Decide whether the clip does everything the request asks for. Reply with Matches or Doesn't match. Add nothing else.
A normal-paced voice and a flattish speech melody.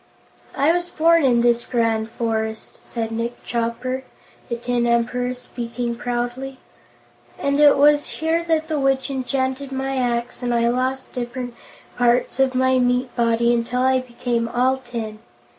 Matches